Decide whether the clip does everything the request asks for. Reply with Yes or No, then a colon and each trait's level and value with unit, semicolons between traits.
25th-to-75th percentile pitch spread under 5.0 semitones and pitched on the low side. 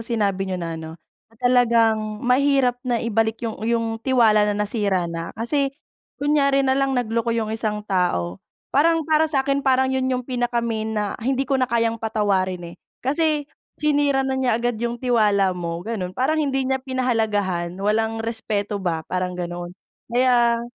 No: average, 4.2 semitones; high, 230 Hz